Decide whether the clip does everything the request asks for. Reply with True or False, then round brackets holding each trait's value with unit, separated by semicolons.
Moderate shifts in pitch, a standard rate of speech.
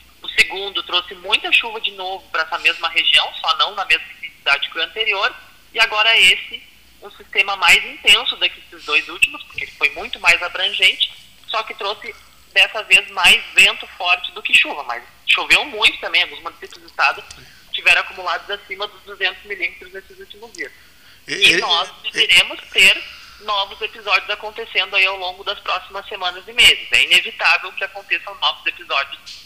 True (3.0 semitones; 175 wpm)